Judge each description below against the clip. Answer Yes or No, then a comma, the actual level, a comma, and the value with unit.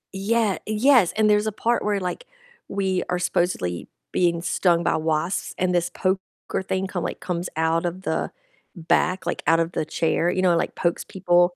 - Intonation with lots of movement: No, narrow, 2.4 semitones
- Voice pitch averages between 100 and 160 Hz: No, medium, 180 Hz